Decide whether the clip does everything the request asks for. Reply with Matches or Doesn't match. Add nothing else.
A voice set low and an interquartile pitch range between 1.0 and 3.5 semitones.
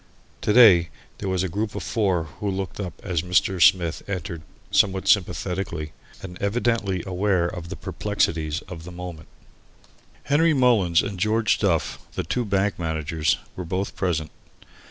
Matches